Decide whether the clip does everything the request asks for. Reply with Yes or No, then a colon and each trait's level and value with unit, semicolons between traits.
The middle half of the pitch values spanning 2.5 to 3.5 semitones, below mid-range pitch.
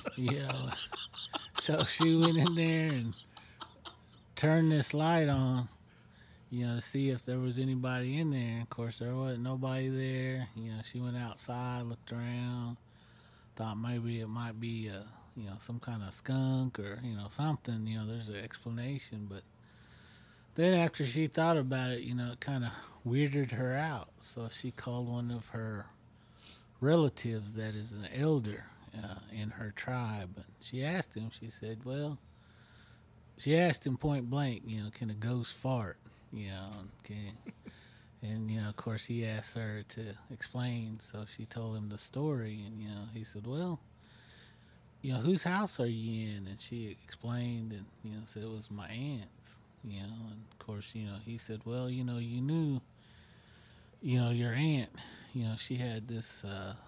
Yes: average, 2.9 semitones; low, 115 Hz